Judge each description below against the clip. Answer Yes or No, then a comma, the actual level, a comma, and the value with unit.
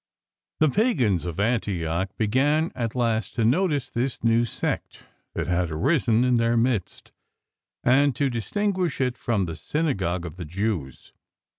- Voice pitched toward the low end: Yes, low, 115 Hz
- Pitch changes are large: Yes, wide, 6.1 semitones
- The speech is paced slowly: No, average, 155 wpm